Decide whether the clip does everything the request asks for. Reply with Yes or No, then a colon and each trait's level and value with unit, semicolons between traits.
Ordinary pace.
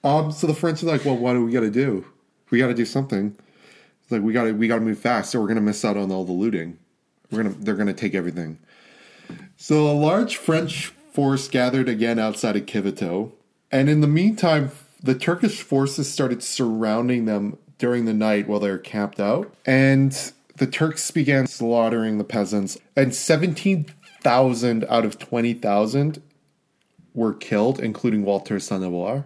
Yes: average, 180 wpm